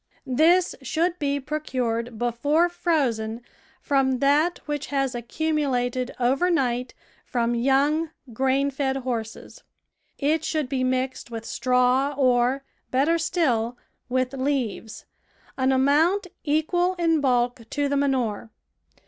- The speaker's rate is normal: No, slow, 120 wpm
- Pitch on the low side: No, very high, 270 Hz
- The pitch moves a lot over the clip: No, average, 3.5 semitones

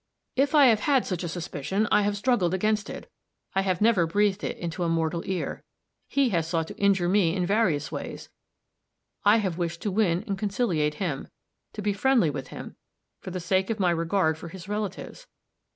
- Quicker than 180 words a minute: Yes, average, 195 wpm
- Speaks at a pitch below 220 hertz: Yes, high, 190 Hz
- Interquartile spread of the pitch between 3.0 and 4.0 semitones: Yes, average, 3.7 semitones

